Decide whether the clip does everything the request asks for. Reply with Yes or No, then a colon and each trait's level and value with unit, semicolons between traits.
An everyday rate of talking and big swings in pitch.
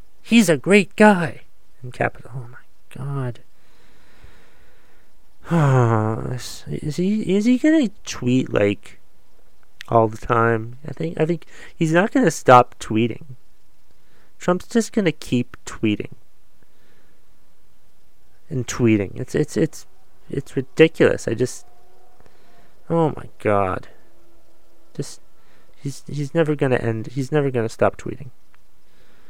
No: slow, 115 wpm; wide, 6.0 semitones